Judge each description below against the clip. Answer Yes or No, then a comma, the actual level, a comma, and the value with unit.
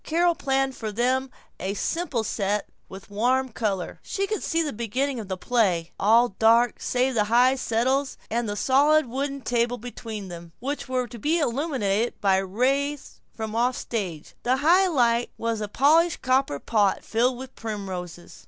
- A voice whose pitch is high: Yes, high, 240 Hz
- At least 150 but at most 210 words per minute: Yes, average, 170 wpm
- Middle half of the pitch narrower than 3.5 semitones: No, average, 4.3 semitones